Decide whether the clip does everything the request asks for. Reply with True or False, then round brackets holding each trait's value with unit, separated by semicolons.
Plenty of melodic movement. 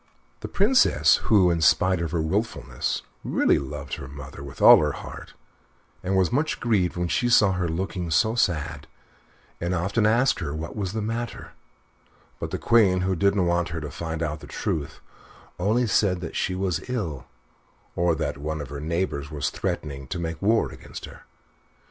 False (4.6 semitones)